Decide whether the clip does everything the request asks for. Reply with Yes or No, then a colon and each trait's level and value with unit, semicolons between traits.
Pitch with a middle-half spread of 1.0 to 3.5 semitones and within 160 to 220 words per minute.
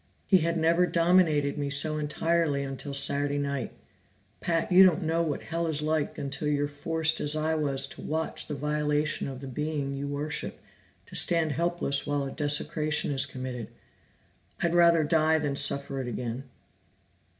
Yes: narrow, 2.5 semitones; average, 165 wpm